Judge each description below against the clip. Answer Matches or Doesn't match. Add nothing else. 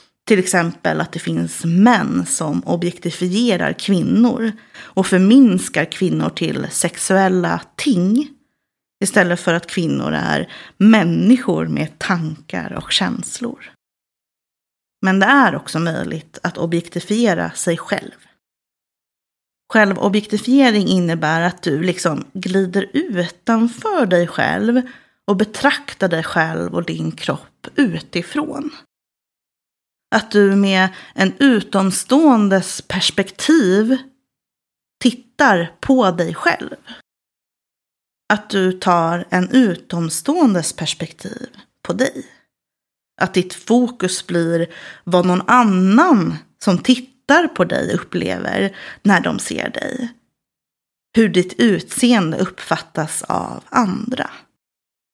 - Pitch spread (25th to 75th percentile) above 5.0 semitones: Matches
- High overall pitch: Matches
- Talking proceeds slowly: Matches